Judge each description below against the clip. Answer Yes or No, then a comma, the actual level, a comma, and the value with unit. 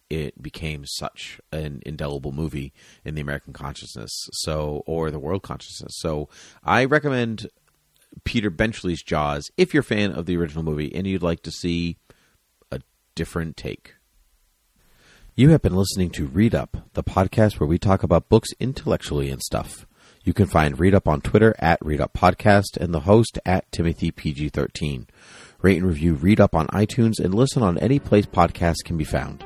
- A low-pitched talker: Yes, very low, 85 Hz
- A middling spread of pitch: Yes, average, 4.7 semitones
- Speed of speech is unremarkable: Yes, average, 180 wpm